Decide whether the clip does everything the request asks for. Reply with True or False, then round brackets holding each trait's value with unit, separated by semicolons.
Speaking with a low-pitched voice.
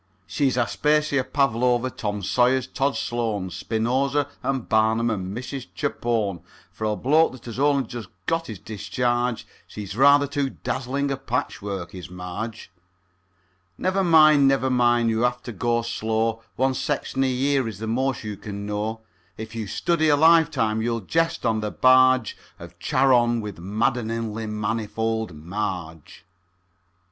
True (120 Hz)